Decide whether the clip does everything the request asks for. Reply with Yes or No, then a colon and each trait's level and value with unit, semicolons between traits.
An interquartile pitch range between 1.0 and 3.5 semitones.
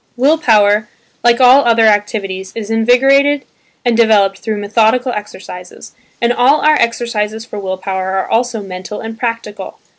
Yes: average, 3.0 semitones